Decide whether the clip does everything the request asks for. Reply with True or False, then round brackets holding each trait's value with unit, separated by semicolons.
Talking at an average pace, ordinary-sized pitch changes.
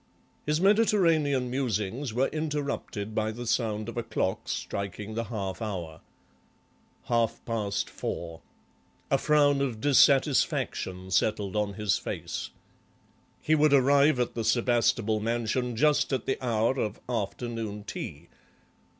False (125 wpm; 4.6 semitones)